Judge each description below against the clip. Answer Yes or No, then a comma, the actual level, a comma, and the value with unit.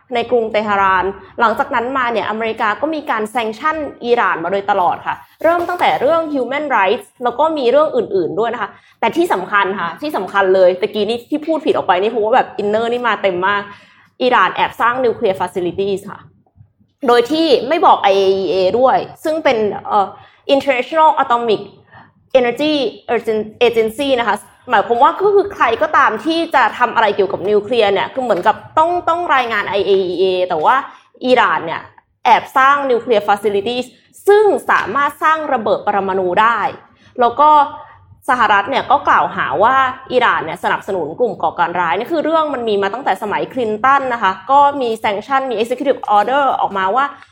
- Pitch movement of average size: No, wide, 6.4 semitones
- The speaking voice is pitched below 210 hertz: No, high, 245 Hz